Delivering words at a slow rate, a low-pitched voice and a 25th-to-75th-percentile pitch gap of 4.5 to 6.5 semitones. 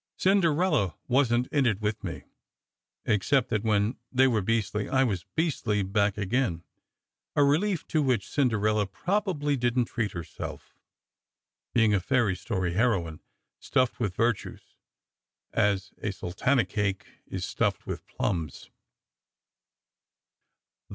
Yes: slow, 130 wpm; low, 110 Hz; average, 4.8 semitones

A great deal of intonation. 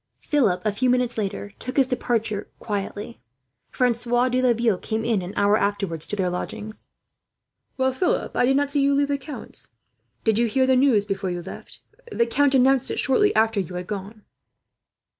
No: average, 4.2 semitones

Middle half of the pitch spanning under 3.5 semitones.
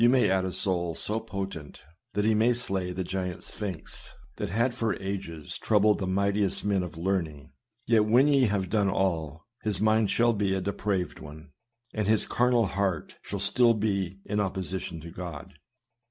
Yes: average, 3.0 semitones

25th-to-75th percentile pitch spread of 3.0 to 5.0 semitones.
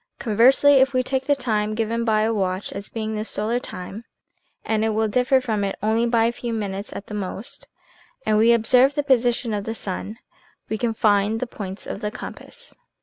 No: narrow, 2.5 semitones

